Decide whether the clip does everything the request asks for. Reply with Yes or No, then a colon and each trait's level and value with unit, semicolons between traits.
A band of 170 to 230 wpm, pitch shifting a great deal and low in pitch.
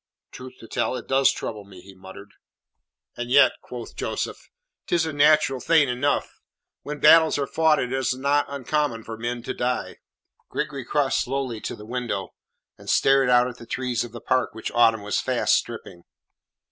No: average, 180 wpm; average, 3.5 semitones; low, 125 Hz